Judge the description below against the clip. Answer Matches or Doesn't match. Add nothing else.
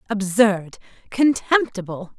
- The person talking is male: Doesn't match